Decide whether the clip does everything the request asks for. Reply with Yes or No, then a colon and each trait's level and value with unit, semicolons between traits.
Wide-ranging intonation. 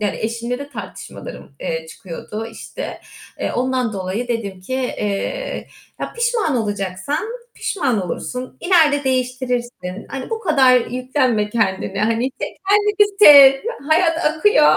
Yes: wide, 6.0 semitones